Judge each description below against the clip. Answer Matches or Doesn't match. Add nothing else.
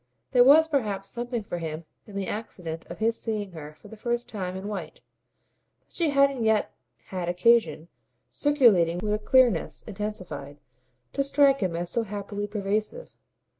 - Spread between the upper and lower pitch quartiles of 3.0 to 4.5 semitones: Doesn't match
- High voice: Matches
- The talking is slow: Doesn't match